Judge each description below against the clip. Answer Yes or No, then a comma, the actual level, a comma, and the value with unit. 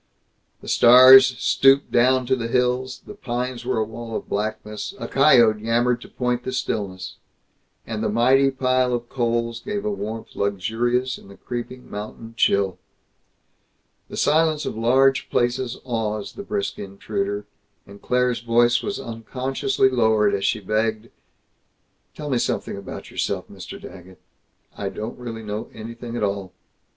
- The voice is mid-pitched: No, low, 120 Hz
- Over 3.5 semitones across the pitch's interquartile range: No, average, 3.0 semitones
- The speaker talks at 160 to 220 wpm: No, average, 150 wpm